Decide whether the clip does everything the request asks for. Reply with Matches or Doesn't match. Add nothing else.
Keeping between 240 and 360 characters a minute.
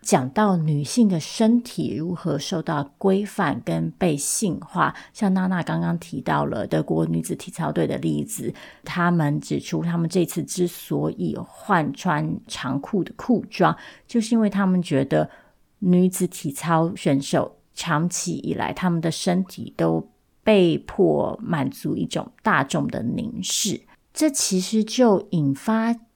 Doesn't match